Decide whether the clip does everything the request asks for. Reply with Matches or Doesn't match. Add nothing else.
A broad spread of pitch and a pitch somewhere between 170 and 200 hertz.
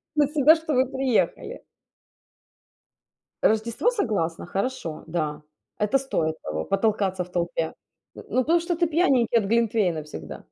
Doesn't match